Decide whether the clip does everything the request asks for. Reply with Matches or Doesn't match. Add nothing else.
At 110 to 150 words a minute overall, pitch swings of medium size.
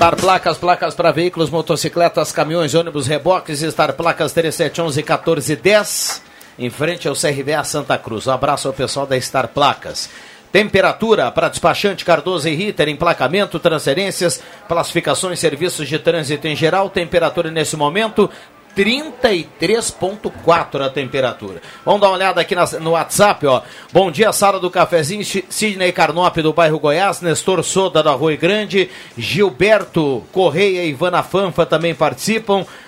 Matches